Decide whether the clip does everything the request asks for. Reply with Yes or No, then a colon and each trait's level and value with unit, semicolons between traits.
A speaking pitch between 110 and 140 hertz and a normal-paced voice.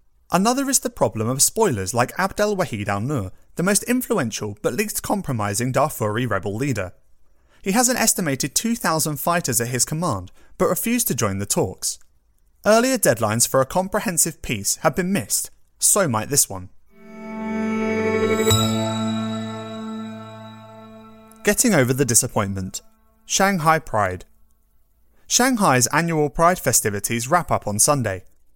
No: low, 135 Hz; slow, 130 wpm